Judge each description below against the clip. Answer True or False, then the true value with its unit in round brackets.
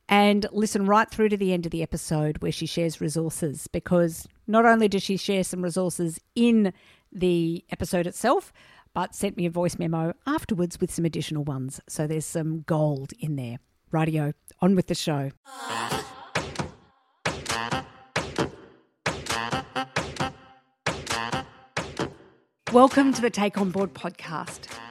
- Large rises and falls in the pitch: True (5.8 semitones)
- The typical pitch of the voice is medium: True (165 Hz)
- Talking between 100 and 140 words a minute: True (135 wpm)